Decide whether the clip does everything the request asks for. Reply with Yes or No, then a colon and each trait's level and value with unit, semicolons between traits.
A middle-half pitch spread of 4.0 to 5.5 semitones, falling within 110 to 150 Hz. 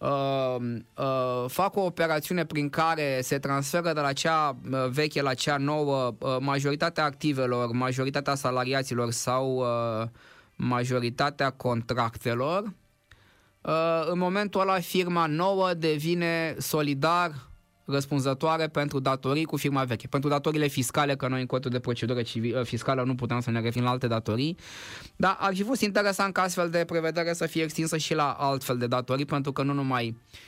Yes: average, 4.3 semitones; medium, 140 Hz